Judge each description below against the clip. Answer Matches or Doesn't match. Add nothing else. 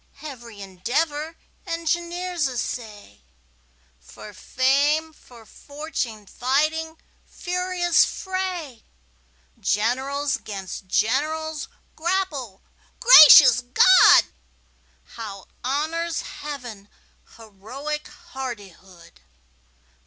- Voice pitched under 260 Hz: Doesn't match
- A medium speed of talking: Doesn't match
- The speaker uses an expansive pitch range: Matches